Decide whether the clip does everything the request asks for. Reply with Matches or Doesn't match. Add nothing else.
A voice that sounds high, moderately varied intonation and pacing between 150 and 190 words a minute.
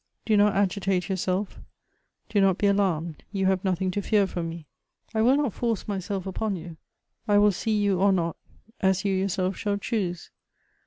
Doesn't match